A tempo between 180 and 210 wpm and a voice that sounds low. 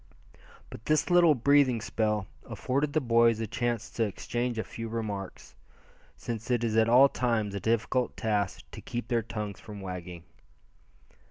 No: average, 160 wpm; low, 115 Hz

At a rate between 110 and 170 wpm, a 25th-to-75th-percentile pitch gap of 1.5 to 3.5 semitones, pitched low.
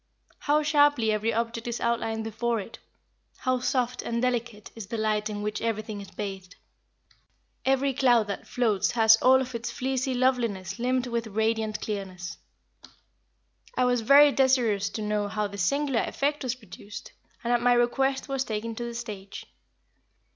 No: average, 165 wpm; average, 3.2 semitones; high, 235 Hz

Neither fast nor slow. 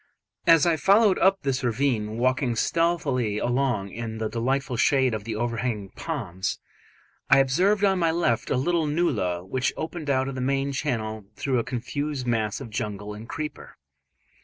Yes: average, 165 wpm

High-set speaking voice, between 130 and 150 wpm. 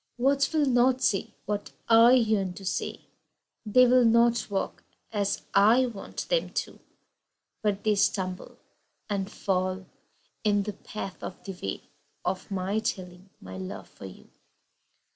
Yes: high, 205 Hz; average, 145 wpm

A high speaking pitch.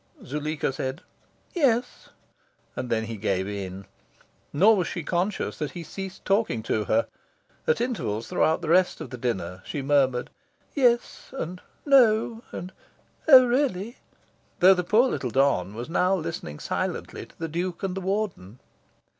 No: medium, 170 Hz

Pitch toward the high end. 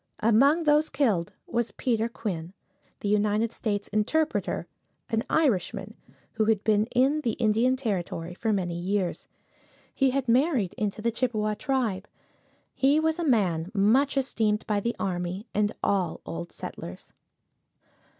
Yes: high, 220 Hz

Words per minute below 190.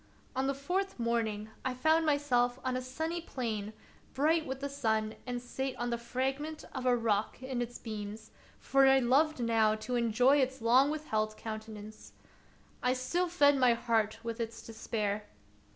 Yes: average, 170 wpm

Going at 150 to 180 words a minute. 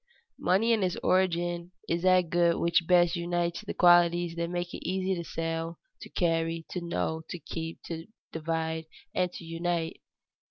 Yes: average, 160 wpm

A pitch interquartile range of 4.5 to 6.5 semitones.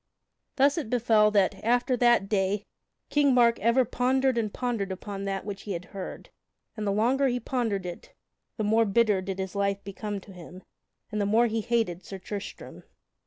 No: average, 3.3 semitones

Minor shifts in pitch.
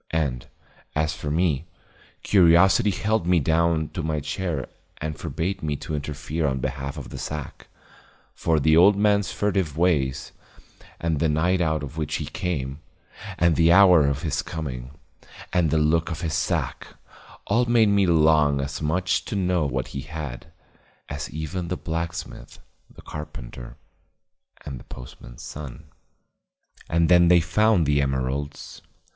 No: average, 3.5 semitones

